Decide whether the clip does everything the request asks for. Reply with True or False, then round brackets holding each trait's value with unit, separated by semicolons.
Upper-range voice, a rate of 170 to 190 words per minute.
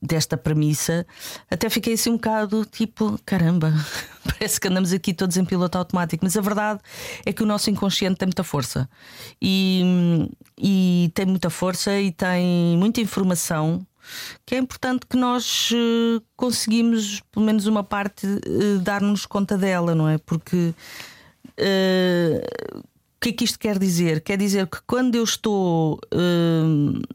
False (195 Hz; 145 wpm)